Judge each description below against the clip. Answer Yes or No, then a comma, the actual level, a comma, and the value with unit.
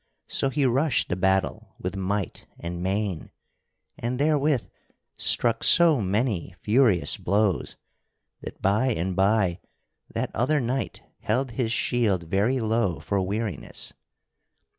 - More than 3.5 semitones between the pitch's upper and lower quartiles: Yes, average, 4.7 semitones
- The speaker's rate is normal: No, slow, 120 wpm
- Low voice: Yes, low, 110 Hz